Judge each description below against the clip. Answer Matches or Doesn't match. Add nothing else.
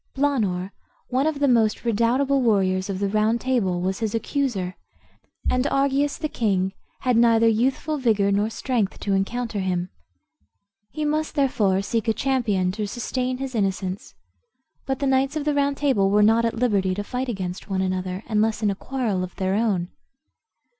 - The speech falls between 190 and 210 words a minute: Doesn't match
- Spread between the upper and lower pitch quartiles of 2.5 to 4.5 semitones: Doesn't match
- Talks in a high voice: Matches